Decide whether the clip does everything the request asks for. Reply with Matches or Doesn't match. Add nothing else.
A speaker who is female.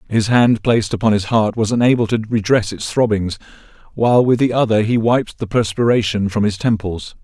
Doesn't match